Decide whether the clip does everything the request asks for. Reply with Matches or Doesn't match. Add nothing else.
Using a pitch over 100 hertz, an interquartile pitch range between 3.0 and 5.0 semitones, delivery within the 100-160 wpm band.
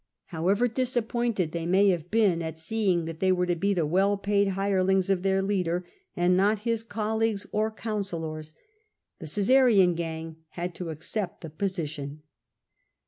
Matches